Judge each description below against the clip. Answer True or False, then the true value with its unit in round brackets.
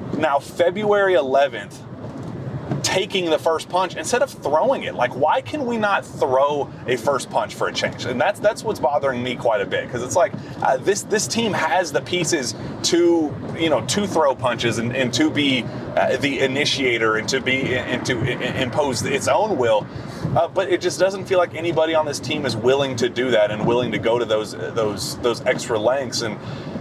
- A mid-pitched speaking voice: True (145 Hz)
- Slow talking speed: False (205 wpm)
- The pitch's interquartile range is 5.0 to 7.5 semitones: True (5.6 semitones)